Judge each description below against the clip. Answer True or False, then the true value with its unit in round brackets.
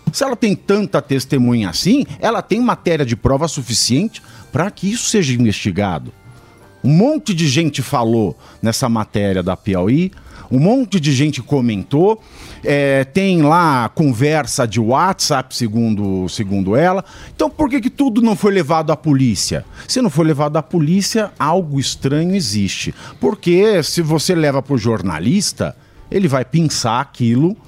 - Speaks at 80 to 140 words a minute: False (150 wpm)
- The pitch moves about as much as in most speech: False (7.6 semitones)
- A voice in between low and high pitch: True (145 Hz)